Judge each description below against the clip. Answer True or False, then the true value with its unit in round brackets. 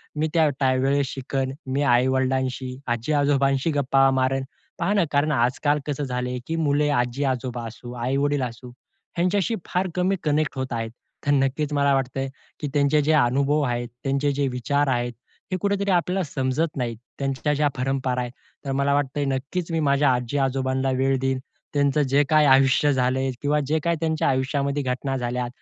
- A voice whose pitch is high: False (135 Hz)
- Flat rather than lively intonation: True (2.1 semitones)